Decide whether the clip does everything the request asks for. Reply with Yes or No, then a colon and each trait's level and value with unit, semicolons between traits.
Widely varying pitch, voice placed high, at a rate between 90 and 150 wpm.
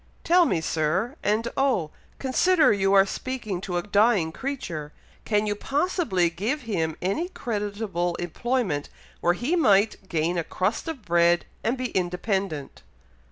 Yes: wide, 6.1 semitones; high, 200 Hz; average, 145 wpm